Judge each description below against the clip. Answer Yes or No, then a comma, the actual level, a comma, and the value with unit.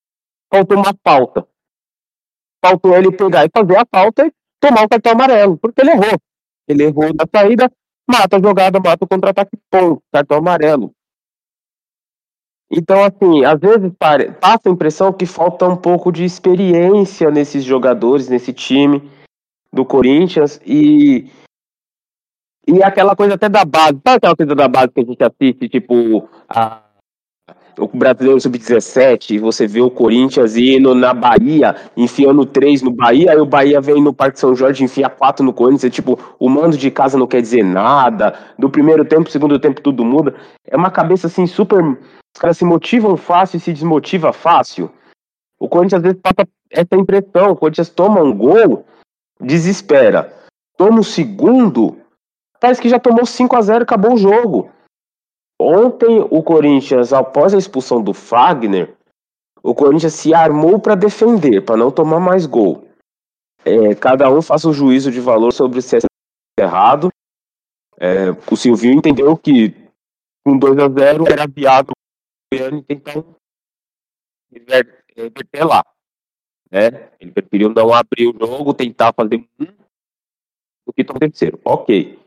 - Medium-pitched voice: Yes, medium, 155 Hz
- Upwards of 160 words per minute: No, average, 155 wpm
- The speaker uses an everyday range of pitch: No, wide, 6.6 semitones